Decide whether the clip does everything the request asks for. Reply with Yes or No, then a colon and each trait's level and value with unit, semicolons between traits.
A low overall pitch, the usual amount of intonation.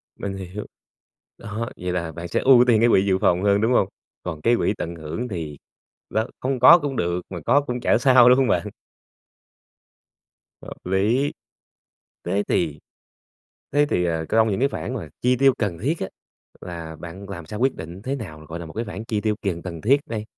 No: low, 105 Hz; wide, 5.9 semitones